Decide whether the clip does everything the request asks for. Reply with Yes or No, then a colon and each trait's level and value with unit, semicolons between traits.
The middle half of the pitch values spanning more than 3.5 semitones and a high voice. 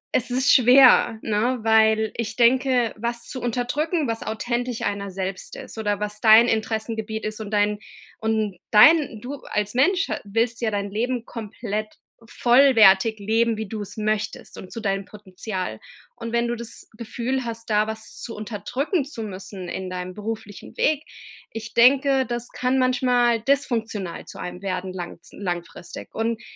No: average, 2.7 semitones; high, 225 Hz